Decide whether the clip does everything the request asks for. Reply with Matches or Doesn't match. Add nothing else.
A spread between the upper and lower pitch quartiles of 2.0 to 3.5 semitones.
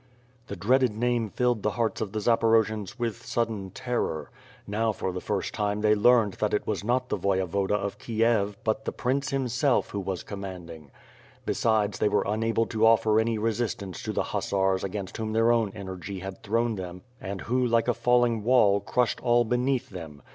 Matches